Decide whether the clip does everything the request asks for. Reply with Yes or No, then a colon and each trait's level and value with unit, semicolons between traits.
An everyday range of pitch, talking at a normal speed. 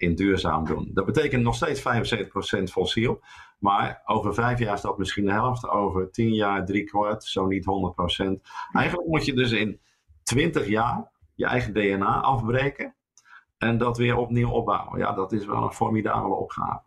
Yes: average, 3.7 semitones; average, 175 wpm